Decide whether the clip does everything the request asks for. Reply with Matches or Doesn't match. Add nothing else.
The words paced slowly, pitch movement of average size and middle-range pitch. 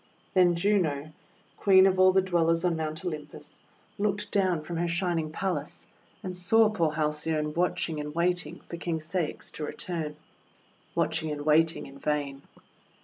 Doesn't match